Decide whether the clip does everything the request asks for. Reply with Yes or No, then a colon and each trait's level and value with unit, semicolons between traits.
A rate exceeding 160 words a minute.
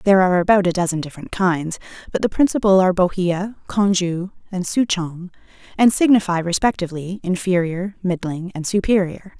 No: average, 140 wpm